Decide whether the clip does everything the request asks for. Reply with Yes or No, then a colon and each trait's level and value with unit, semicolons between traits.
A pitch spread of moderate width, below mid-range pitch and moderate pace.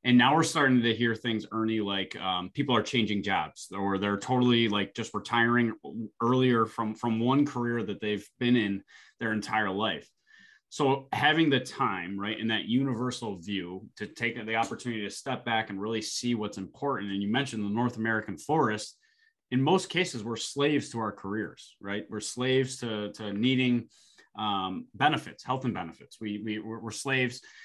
Yes: average, 3.2 semitones; low, 115 Hz; average, 180 wpm